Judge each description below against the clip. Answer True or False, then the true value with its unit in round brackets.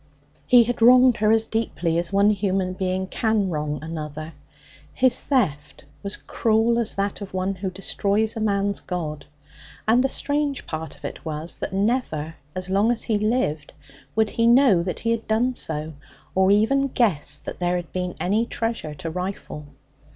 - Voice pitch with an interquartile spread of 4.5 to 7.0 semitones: True (4.9 semitones)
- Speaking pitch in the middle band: False (200 Hz)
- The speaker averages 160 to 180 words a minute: True (175 wpm)